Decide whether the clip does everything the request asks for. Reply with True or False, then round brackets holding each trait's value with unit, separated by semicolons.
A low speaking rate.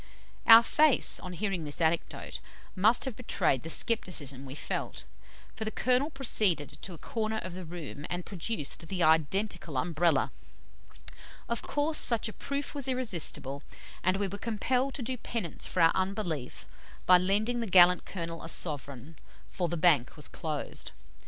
False (160 wpm)